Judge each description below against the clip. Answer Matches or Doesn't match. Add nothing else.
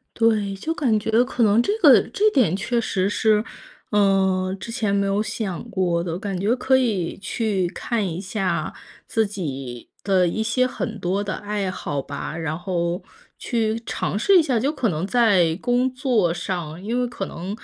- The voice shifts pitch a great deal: Doesn't match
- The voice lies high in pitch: Matches